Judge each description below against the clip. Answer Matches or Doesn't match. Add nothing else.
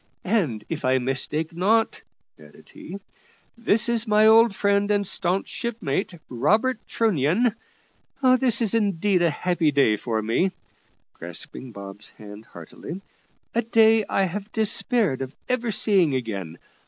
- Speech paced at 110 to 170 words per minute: Matches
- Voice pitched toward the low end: Doesn't match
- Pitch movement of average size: Doesn't match